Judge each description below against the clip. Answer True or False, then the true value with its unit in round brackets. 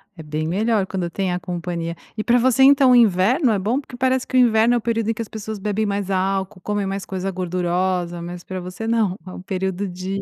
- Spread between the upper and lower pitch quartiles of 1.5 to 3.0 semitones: False (3.6 semitones)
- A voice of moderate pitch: False (195 Hz)